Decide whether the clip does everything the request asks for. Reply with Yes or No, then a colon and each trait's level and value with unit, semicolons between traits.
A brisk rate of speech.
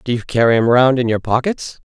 Yes: fast, 255 wpm